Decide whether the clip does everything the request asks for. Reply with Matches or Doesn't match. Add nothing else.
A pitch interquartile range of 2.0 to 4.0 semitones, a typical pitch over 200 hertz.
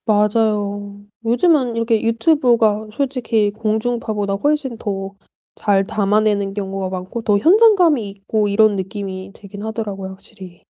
Matches